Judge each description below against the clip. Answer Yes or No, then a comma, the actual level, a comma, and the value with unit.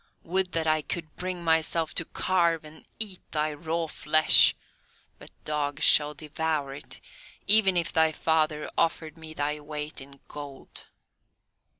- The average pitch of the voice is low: No, medium, 155 Hz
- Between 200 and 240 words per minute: No, average, 140 wpm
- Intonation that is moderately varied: No, narrow, 1.8 semitones